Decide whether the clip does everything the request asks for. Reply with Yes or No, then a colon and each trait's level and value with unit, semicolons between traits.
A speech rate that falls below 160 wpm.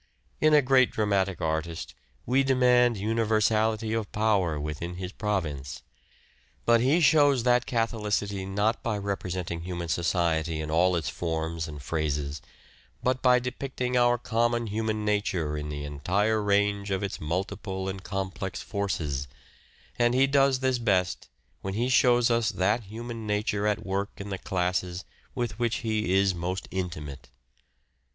Yes: average, 145 wpm